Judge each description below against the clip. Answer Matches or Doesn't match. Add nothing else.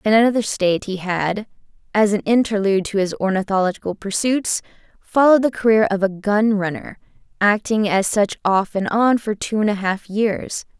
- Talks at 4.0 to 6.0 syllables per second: Matches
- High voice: Matches